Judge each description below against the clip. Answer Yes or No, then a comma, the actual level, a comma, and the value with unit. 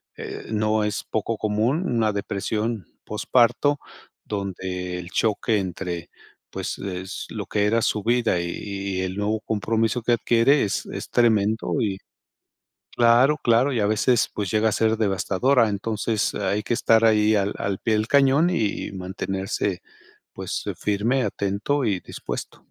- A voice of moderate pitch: No, low, 105 Hz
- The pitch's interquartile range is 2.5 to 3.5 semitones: Yes, average, 2.8 semitones